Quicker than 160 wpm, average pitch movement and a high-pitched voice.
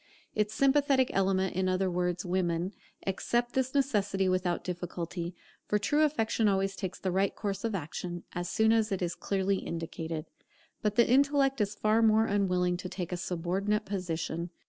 Yes: average, 170 wpm; average, 3.6 semitones; high, 195 Hz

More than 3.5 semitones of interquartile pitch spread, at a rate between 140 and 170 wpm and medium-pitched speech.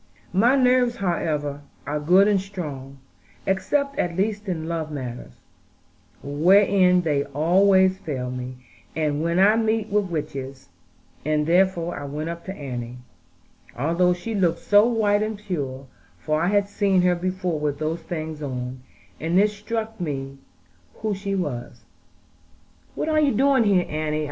Yes: wide, 5.4 semitones; average, 150 wpm; medium, 175 Hz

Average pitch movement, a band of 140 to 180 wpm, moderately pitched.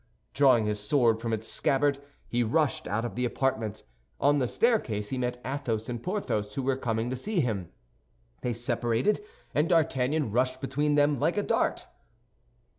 No: average, 4.2 semitones; average, 170 wpm; low, 125 Hz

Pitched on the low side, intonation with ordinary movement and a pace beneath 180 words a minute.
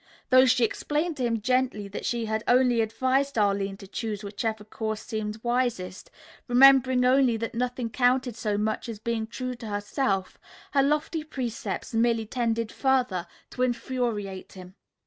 No: high, 235 Hz; average, 3.1 semitones; average, 155 wpm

